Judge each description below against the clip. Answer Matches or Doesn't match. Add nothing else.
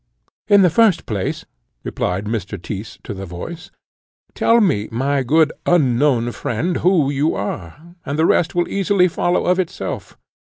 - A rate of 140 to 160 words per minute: Matches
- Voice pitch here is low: Doesn't match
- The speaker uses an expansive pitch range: Matches